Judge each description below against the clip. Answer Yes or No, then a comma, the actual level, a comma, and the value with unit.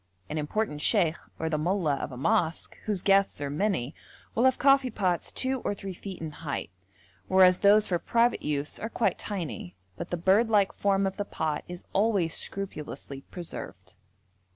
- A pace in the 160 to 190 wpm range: Yes, average, 175 wpm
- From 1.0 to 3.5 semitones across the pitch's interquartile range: No, average, 4.9 semitones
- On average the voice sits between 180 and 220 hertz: Yes, high, 190 Hz